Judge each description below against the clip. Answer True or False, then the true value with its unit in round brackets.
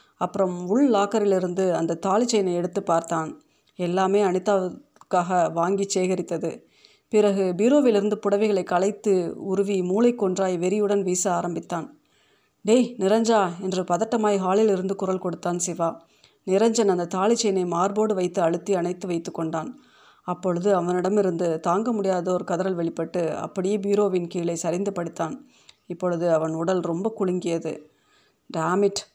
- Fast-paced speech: False (115 wpm)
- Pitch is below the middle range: False (190 Hz)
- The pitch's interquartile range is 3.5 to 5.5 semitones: False (2.7 semitones)